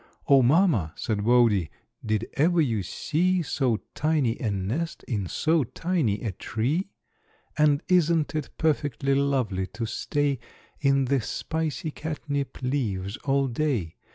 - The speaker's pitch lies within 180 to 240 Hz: No, low, 135 Hz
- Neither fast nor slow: No, slow, 130 wpm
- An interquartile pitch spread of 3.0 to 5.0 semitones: No, wide, 5.6 semitones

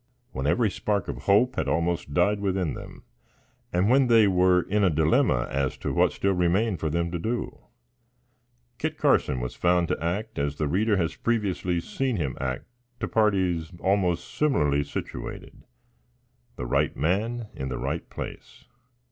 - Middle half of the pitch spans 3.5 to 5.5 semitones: Yes, average, 5.0 semitones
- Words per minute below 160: No, average, 165 wpm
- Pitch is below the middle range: Yes, very low, 90 Hz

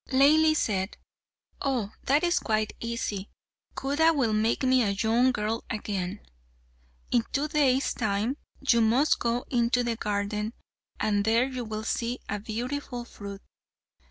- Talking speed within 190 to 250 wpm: No, average, 140 wpm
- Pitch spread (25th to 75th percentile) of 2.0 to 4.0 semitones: Yes, average, 3.6 semitones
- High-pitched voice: Yes, high, 235 Hz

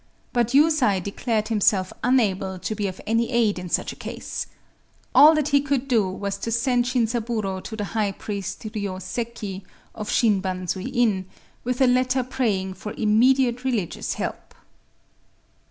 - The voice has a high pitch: Yes, high, 220 Hz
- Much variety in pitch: No, average, 4.1 semitones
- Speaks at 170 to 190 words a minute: No, average, 155 wpm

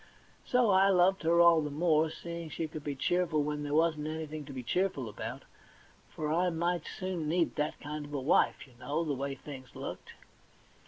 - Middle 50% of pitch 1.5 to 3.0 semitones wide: Yes, average, 2.7 semitones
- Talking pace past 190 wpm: Yes, average, 200 wpm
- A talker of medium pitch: Yes, medium, 155 Hz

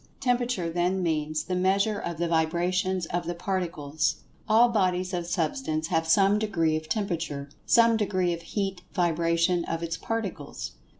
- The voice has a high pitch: No, medium, 175 Hz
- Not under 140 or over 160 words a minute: Yes, average, 145 wpm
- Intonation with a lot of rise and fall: No, average, 3.2 semitones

